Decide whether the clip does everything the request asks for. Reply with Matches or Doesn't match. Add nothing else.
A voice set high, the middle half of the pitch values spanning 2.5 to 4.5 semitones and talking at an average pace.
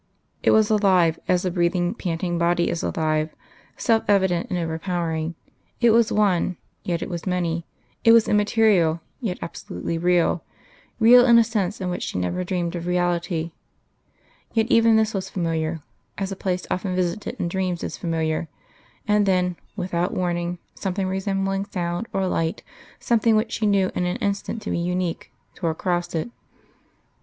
Doesn't match